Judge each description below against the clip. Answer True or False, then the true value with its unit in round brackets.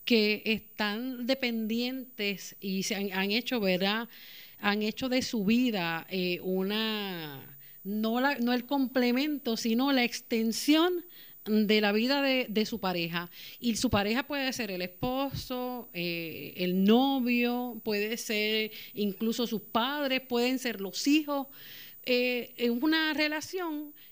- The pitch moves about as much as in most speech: True (3.9 semitones)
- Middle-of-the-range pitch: False (230 Hz)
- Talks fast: False (135 wpm)